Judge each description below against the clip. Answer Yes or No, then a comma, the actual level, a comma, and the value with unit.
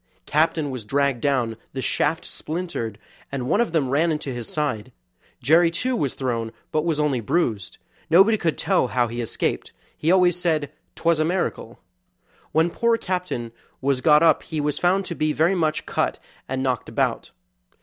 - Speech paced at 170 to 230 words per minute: Yes, average, 175 wpm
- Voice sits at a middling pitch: Yes, medium, 150 Hz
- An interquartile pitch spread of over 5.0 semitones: No, average, 4.7 semitones